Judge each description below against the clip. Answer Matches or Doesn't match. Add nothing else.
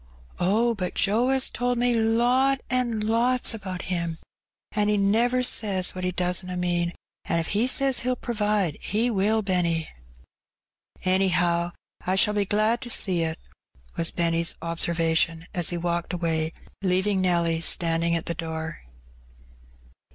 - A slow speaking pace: Doesn't match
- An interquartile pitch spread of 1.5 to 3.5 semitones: Doesn't match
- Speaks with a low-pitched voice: Doesn't match